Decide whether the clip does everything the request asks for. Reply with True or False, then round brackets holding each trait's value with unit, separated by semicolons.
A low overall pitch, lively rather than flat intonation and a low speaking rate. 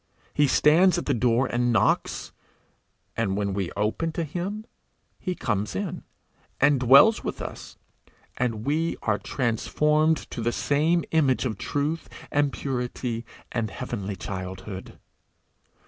True (125 Hz; 5.7 semitones; 130 wpm)